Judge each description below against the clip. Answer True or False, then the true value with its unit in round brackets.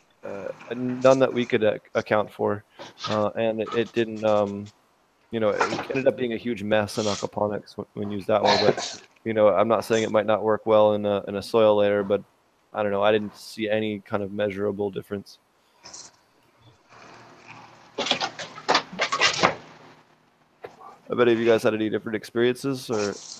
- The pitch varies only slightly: True (1.6 semitones)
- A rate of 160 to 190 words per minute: True (180 wpm)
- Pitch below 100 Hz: False (105 Hz)